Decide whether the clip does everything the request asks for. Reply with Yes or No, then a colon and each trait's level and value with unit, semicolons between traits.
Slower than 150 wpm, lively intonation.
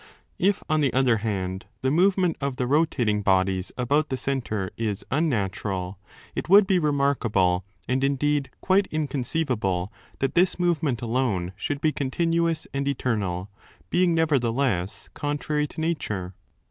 Yes: average, 140 wpm; wide, 6.9 semitones